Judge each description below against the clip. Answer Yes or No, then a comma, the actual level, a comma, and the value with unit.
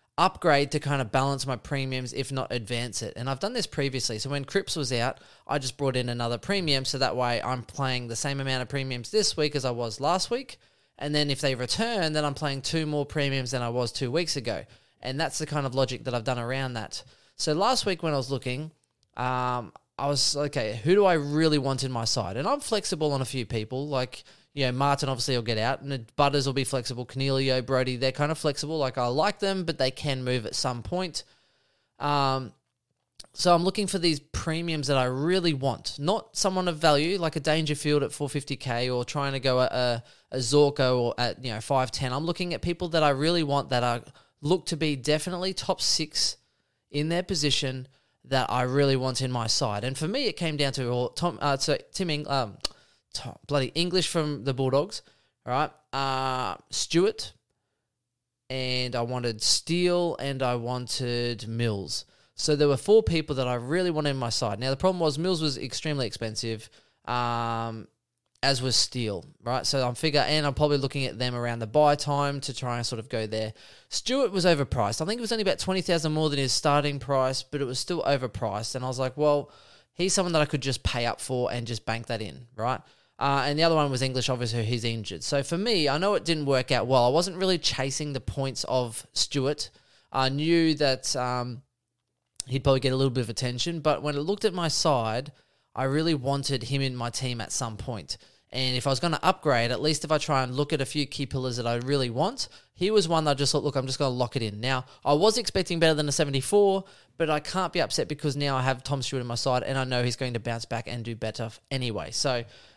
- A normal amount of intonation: Yes, average, 3.4 semitones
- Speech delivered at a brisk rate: Yes, fast, 230 wpm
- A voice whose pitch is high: No, low, 135 Hz